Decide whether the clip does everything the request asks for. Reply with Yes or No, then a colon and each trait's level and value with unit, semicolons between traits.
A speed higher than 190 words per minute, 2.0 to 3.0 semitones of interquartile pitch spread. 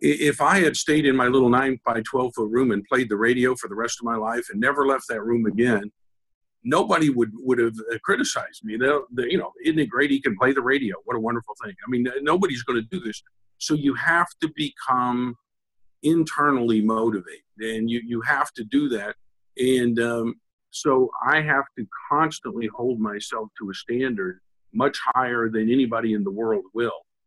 Yes: average, 200 wpm; average, 2.7 semitones